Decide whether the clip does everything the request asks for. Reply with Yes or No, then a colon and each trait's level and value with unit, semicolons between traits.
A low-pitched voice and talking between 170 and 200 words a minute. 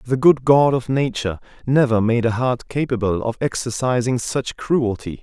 No: low, 120 Hz; average, 160 wpm